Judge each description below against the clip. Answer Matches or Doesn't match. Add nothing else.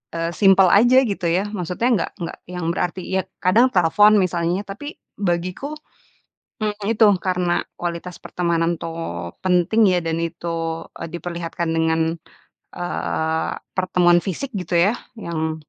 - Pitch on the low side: Doesn't match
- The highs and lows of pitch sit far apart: Doesn't match